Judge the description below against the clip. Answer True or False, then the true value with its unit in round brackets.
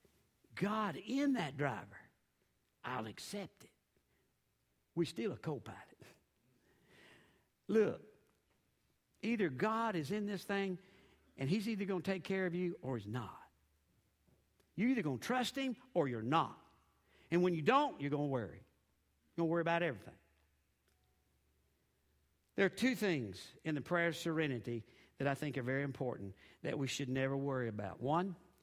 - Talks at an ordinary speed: True (155 wpm)